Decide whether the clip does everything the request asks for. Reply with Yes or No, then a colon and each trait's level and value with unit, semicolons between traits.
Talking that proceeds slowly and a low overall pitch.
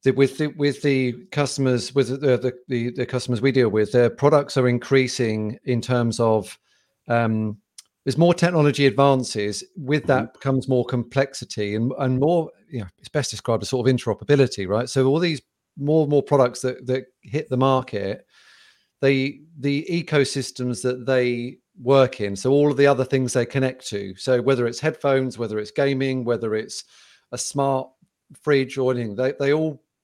No: average, 180 wpm; low, 130 Hz